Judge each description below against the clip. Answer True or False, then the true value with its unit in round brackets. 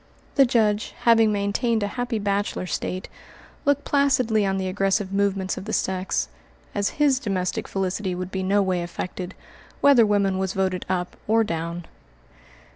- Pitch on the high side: True (200 Hz)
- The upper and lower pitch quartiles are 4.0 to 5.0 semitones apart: False (3.0 semitones)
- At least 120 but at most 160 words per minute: True (155 wpm)